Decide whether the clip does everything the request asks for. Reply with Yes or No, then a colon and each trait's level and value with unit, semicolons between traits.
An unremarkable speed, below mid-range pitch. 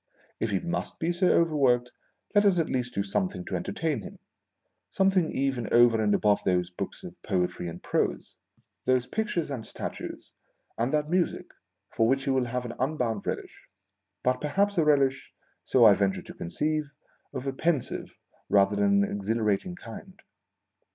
Yes: average, 170 wpm; low, 125 Hz